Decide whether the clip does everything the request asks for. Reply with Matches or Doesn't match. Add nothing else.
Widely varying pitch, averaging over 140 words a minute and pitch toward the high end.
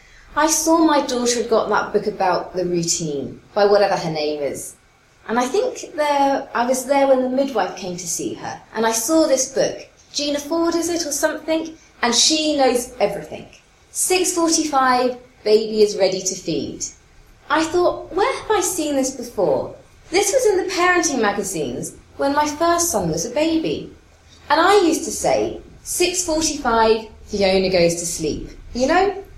Matches